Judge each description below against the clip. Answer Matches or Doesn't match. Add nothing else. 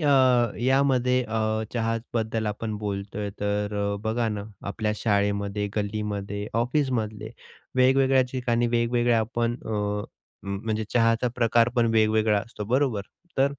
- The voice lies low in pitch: Matches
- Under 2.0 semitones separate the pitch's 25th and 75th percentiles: Doesn't match